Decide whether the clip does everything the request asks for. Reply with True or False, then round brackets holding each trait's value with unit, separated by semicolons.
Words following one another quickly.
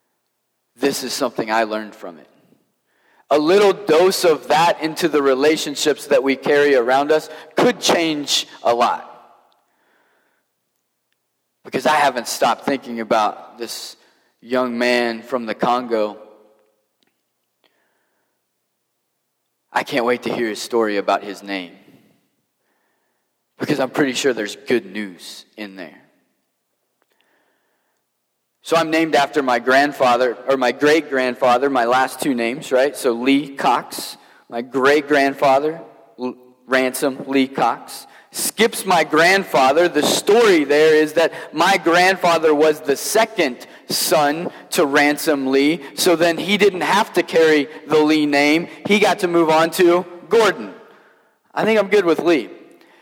False (135 wpm)